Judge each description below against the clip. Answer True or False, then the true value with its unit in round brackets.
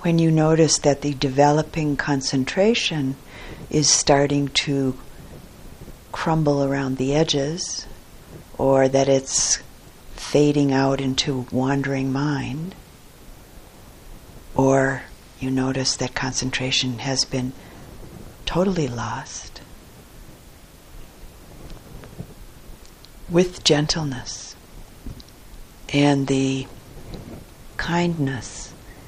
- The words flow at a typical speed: False (75 wpm)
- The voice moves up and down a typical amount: False (2.1 semitones)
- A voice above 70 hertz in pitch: True (135 Hz)